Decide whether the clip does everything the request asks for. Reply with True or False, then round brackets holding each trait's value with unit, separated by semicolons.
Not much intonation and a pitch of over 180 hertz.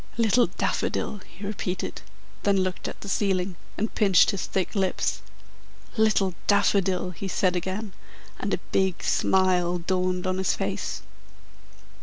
True (1.7 semitones; 190 Hz)